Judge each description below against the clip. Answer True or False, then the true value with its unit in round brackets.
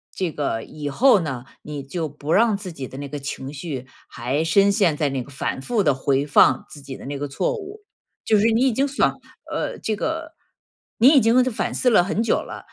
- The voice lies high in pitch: False (160 Hz)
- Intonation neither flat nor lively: False (8.4 semitones)